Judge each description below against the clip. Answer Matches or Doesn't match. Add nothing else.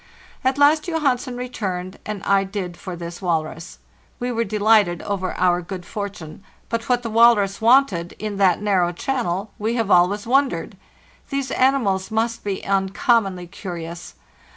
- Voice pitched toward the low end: Doesn't match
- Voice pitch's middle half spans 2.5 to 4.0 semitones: Doesn't match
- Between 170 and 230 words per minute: Doesn't match